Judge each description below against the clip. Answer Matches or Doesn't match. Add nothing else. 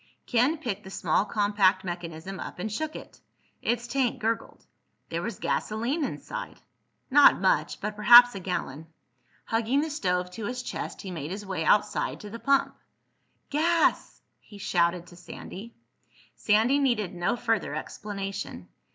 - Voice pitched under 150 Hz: Doesn't match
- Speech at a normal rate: Matches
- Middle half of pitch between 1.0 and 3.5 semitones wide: Doesn't match